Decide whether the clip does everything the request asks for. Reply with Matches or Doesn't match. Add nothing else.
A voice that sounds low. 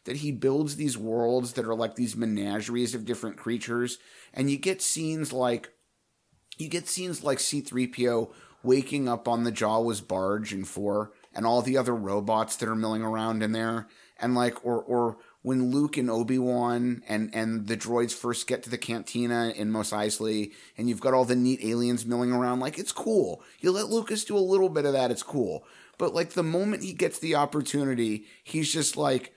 Matches